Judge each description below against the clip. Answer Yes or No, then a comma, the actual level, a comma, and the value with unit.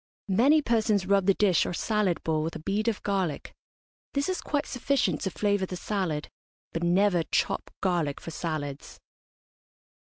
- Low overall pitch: No, high, 190 Hz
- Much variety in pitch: No, average, 4.1 semitones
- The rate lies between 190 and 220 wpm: No, average, 160 wpm